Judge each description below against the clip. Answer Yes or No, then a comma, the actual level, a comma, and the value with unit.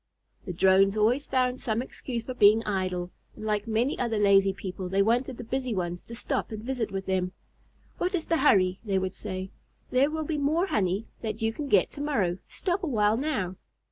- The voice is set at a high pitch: Yes, high, 220 Hz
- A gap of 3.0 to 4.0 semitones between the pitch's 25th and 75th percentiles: No, average, 5.2 semitones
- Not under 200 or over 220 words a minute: Yes, fast, 205 wpm